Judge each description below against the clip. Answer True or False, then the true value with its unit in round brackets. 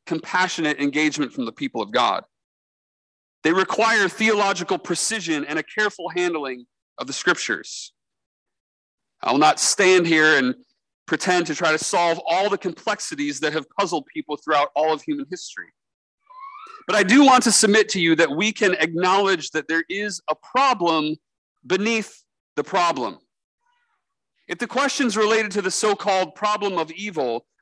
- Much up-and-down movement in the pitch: True (5.9 semitones)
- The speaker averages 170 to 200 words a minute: False (155 wpm)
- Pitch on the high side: True (195 Hz)